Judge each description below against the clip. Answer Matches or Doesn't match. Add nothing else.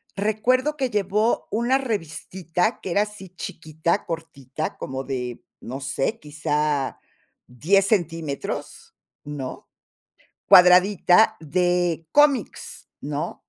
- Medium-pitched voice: Matches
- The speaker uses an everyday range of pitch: Doesn't match